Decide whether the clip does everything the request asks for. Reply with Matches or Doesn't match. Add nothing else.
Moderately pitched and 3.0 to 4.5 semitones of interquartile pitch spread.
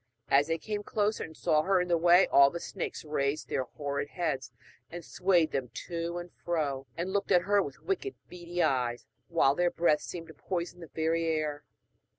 Matches